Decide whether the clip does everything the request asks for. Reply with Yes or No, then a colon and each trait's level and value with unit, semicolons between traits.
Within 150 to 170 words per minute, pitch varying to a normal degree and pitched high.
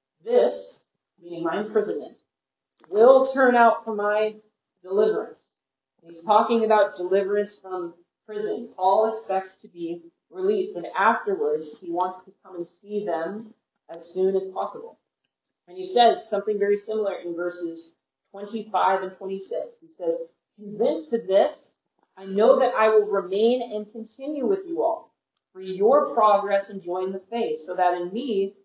Yes: average, 155 wpm; average, 3.7 semitones; high, 205 Hz